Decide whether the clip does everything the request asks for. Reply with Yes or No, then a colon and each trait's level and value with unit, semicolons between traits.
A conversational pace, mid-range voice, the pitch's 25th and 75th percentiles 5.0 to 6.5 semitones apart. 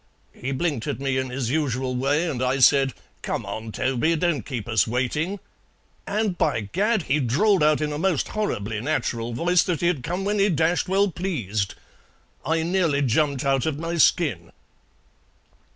Yes: average, 170 wpm; medium, 145 Hz; wide, 5.5 semitones